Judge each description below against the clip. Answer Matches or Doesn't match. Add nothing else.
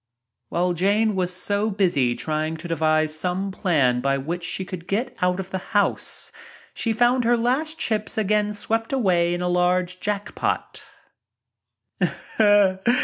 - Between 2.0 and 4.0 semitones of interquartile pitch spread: Matches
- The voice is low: Doesn't match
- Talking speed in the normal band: Matches